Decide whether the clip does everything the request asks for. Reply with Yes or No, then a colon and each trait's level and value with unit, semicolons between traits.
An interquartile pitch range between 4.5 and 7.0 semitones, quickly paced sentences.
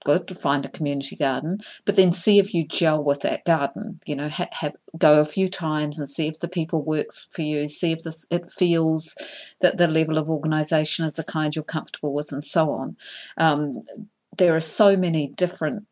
No: average, 2.7 semitones; fast, 210 wpm